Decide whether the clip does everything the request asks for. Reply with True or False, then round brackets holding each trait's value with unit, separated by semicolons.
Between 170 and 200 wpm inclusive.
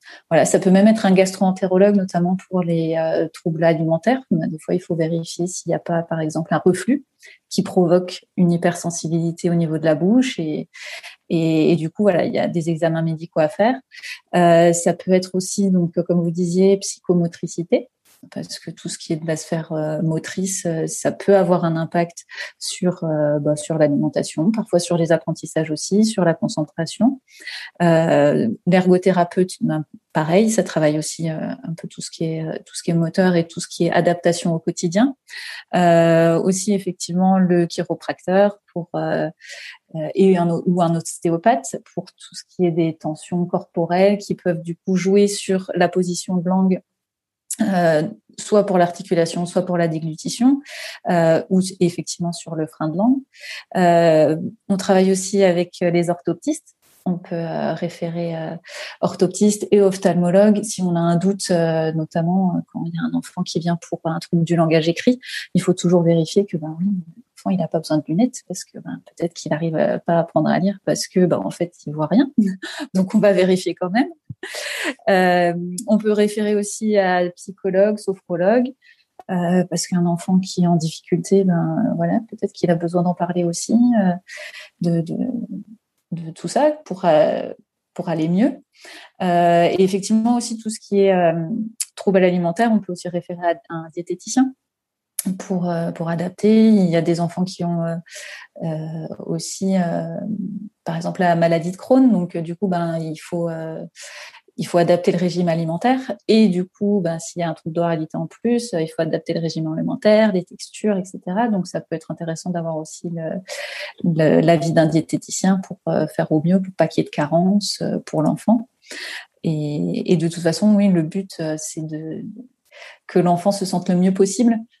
True (185 wpm)